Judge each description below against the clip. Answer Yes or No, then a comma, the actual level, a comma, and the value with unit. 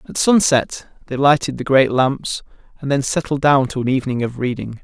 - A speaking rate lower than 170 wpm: No, average, 200 wpm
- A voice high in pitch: No, low, 135 Hz